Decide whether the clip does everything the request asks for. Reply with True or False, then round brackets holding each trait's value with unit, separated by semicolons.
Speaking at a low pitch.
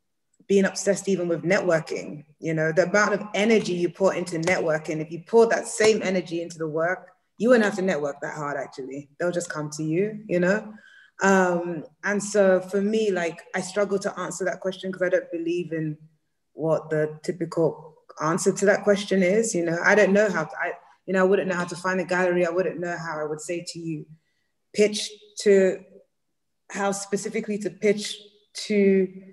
False (185 Hz)